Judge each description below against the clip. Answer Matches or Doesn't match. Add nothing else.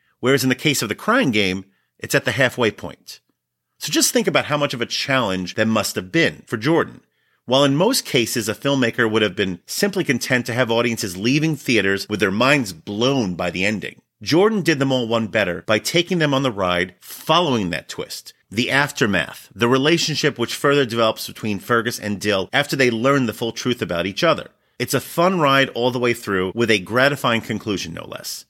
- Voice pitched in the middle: Doesn't match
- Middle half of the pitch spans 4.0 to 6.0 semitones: Matches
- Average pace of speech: Doesn't match